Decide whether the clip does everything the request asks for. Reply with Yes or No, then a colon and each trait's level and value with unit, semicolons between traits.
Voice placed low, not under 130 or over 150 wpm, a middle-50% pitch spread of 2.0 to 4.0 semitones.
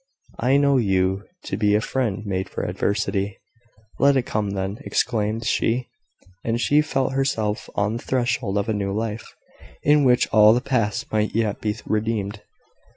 No: low, 110 Hz; average, 165 wpm; average, 3.2 semitones